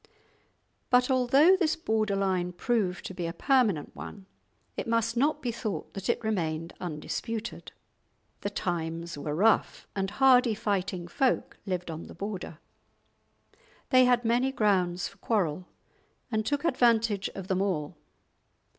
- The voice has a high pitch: Yes, high, 205 Hz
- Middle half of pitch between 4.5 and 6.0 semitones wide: Yes, average, 5.2 semitones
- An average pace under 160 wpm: Yes, average, 140 wpm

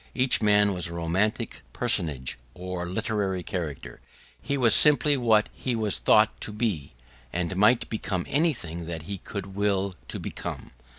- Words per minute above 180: No, average, 155 wpm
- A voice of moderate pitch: No, low, 100 Hz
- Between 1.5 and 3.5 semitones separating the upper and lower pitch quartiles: No, average, 4.1 semitones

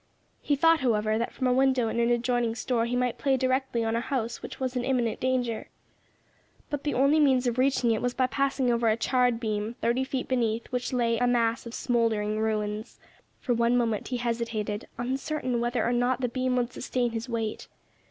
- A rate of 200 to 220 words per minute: Yes, fast, 205 wpm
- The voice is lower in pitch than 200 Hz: No, high, 240 Hz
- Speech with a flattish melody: Yes, narrow, 2.0 semitones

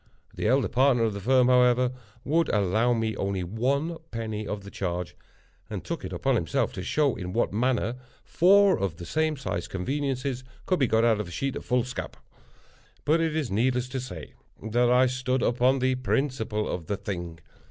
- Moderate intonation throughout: Yes, average, 4.1 semitones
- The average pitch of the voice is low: Yes, low, 125 Hz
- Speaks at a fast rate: No, average, 190 wpm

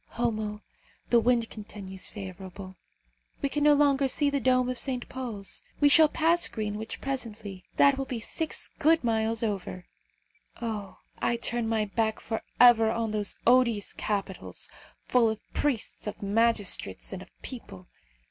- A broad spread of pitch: No, average, 3.5 semitones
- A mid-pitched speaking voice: No, high, 230 Hz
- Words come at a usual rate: Yes, average, 150 wpm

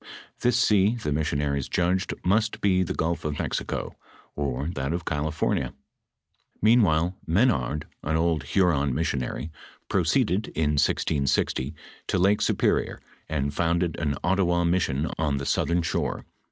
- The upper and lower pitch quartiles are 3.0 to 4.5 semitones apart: Yes, average, 4.2 semitones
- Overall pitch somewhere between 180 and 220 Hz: No, very low, 80 Hz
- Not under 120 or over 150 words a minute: Yes, average, 140 wpm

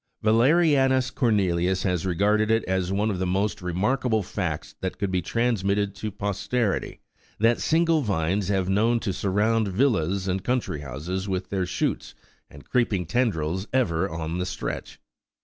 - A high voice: No, low, 100 Hz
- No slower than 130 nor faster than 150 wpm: No, average, 160 wpm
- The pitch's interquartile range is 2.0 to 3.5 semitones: No, average, 3.9 semitones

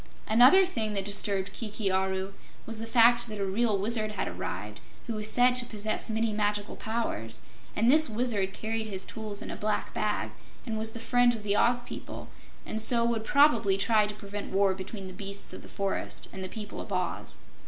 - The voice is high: Yes, high, 215 Hz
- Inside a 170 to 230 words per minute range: Yes, fast, 205 wpm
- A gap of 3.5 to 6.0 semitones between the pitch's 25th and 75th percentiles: No, narrow, 2.6 semitones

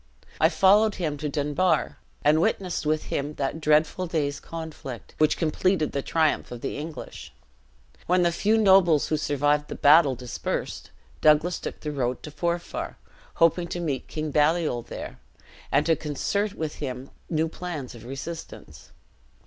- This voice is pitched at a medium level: Yes, medium, 155 Hz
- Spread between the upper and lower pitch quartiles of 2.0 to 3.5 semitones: Yes, average, 2.9 semitones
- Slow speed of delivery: No, average, 155 wpm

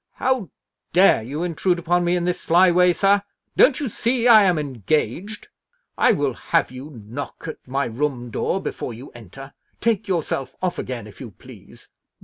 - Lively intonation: Yes, wide, 6.6 semitones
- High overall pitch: No, medium, 170 Hz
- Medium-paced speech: Yes, average, 175 wpm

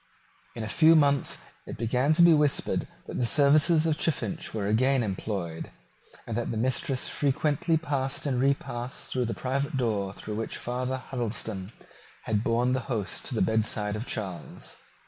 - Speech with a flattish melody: No, average, 4.3 semitones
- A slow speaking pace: No, average, 165 wpm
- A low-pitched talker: Yes, low, 125 Hz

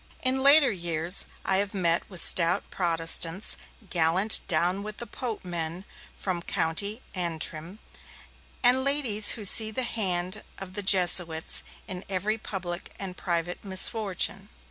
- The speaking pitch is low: No, high, 190 Hz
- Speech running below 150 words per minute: Yes, slow, 135 wpm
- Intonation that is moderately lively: Yes, average, 3.5 semitones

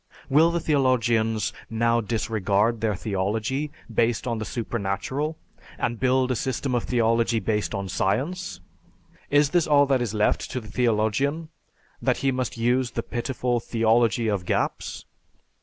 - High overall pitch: No, low, 115 Hz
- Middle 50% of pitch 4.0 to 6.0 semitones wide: No, average, 3.2 semitones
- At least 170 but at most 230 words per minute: No, average, 150 wpm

